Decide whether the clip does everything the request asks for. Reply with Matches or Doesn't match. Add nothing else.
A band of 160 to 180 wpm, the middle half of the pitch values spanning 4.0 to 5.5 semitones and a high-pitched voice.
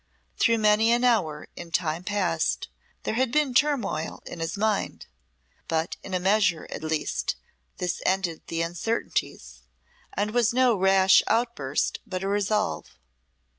Doesn't match